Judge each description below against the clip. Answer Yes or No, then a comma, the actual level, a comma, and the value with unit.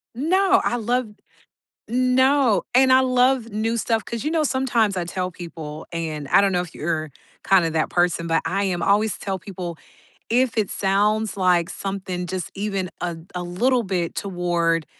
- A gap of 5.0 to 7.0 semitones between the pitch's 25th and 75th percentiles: Yes, wide, 5.5 semitones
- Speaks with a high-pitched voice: Yes, high, 195 Hz